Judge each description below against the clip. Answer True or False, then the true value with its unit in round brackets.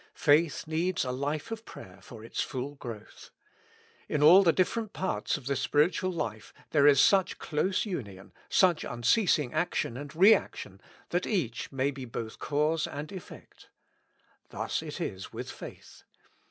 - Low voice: False (150 Hz)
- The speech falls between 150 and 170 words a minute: True (155 wpm)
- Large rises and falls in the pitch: True (6.1 semitones)